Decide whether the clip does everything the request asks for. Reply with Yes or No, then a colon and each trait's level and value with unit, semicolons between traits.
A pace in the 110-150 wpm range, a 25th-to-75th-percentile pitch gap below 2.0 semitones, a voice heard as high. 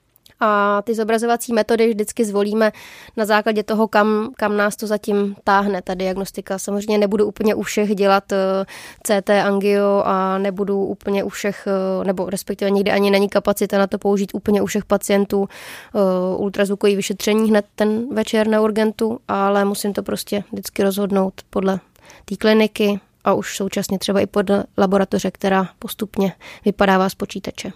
No: average, 160 wpm; narrow, 1.3 semitones; high, 205 Hz